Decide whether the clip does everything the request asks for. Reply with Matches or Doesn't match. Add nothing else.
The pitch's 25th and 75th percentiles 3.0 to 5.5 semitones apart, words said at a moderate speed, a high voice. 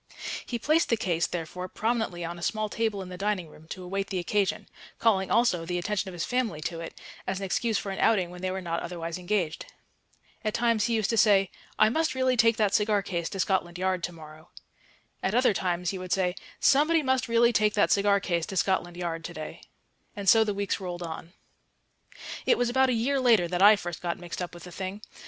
Doesn't match